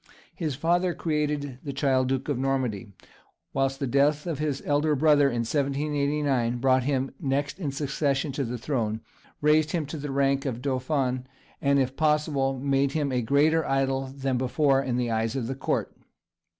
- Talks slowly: No, average, 175 wpm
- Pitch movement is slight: Yes, narrow, 2.2 semitones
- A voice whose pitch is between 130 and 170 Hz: Yes, low, 135 Hz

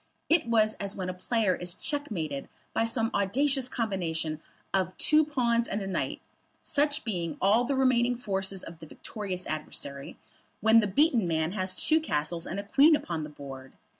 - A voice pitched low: No, high, 200 Hz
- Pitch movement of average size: No, wide, 5.8 semitones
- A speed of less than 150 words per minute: No, average, 175 wpm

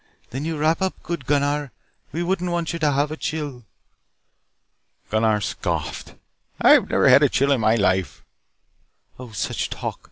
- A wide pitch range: Yes, wide, 5.7 semitones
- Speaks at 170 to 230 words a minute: No, average, 160 wpm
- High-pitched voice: No, medium, 145 Hz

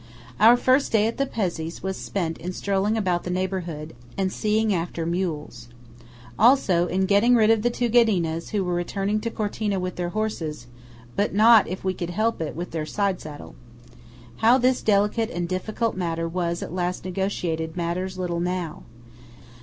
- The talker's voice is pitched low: No, medium, 185 Hz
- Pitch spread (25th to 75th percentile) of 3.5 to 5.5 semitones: Yes, average, 3.9 semitones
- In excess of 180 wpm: No, average, 175 wpm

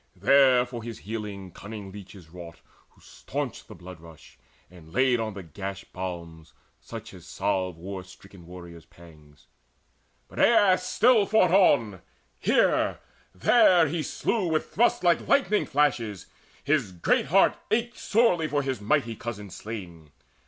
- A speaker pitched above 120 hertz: No, low, 105 Hz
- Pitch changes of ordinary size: No, wide, 8.6 semitones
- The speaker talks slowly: No, average, 145 wpm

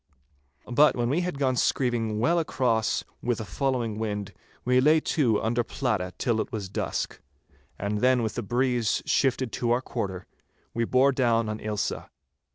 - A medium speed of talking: Yes, average, 165 wpm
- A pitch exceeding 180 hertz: No, low, 120 Hz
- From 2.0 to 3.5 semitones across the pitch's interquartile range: Yes, average, 3.0 semitones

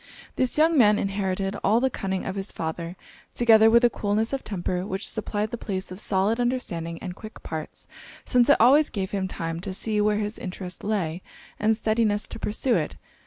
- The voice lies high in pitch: Yes, high, 205 Hz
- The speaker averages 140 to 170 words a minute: No, average, 195 wpm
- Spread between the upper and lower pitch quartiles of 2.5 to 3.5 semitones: Yes, average, 3.1 semitones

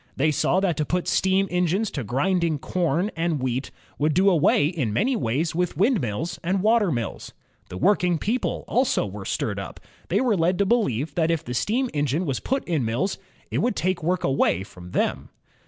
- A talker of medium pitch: Yes, medium, 170 Hz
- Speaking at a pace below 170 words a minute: No, average, 195 wpm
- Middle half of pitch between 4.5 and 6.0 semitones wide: Yes, average, 5.3 semitones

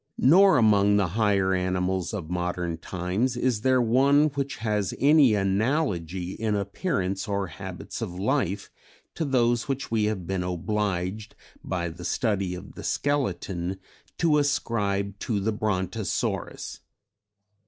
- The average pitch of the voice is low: Yes, low, 100 Hz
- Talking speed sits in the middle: No, slow, 130 wpm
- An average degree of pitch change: Yes, average, 4.7 semitones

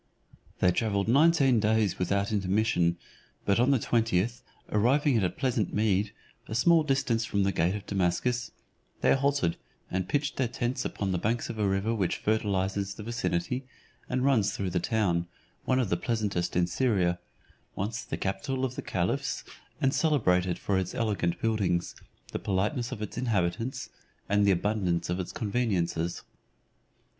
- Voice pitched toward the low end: Yes, low, 105 Hz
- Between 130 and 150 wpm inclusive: No, average, 160 wpm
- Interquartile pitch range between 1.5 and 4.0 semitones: No, average, 4.6 semitones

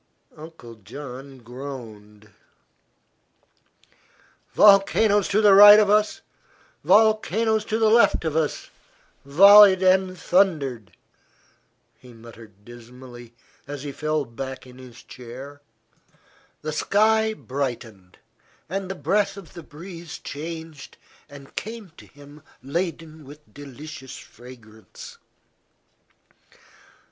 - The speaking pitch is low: No, medium, 150 Hz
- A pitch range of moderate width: No, wide, 7.4 semitones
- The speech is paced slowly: Yes, slow, 95 wpm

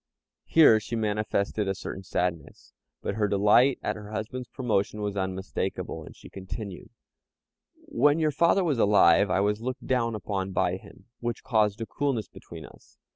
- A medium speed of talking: Yes, average, 165 wpm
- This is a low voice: Yes, low, 105 Hz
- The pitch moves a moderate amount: Yes, average, 3.5 semitones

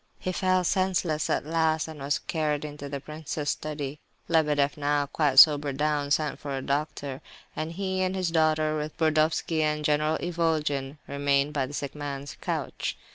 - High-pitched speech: No, medium, 150 Hz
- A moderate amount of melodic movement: No, narrow, 1.8 semitones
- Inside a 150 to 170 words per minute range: Yes, average, 165 wpm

